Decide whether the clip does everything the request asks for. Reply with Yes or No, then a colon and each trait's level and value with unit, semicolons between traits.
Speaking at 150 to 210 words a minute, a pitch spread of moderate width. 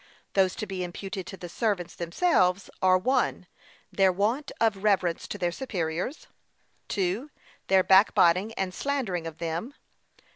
No: average, 140 wpm; average, 3.3 semitones